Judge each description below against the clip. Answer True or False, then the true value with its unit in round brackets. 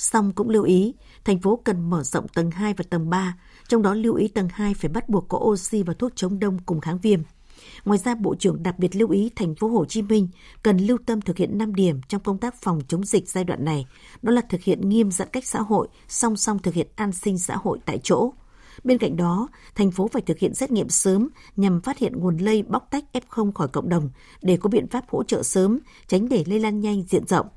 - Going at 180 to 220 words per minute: False (250 wpm)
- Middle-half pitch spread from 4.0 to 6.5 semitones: False (3.4 semitones)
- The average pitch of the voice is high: True (205 Hz)